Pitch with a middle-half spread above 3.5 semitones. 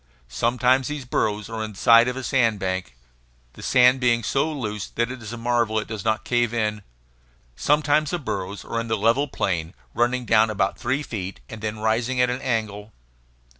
No: average, 2.8 semitones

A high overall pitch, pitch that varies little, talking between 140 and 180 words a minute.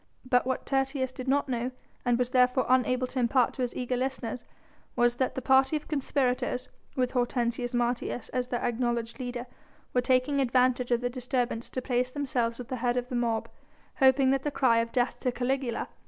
No: very high, 250 Hz; narrow, 1.3 semitones; average, 195 wpm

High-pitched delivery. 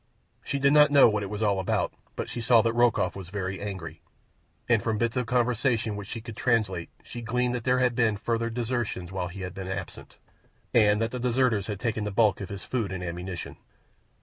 No: low, 110 Hz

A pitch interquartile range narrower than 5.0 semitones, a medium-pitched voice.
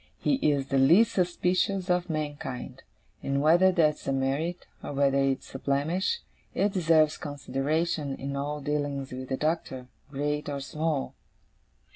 Yes: average, 3.6 semitones; medium, 150 Hz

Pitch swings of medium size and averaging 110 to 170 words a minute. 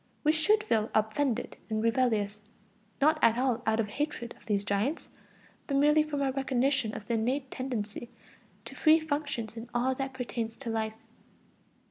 Yes: average, 4.2 semitones; average, 165 wpm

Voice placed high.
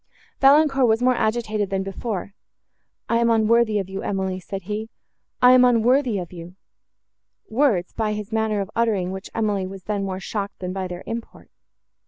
Yes: high, 210 Hz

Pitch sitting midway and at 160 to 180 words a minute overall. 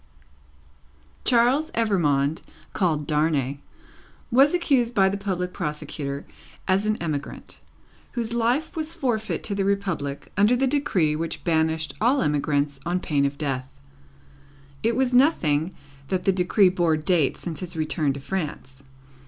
No: medium, 180 Hz; slow, 135 wpm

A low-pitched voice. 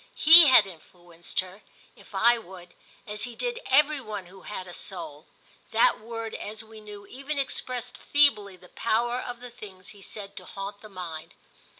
No: high, 210 Hz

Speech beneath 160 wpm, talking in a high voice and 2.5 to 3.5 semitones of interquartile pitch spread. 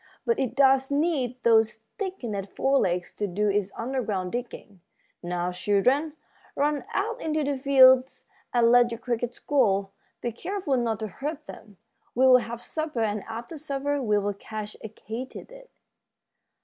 No: average, 150 wpm; high, 245 Hz; average, 4.8 semitones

